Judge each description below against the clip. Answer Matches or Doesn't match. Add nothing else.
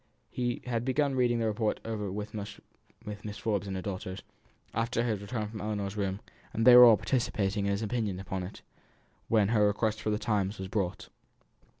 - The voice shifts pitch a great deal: Doesn't match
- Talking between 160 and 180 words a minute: Doesn't match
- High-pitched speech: Doesn't match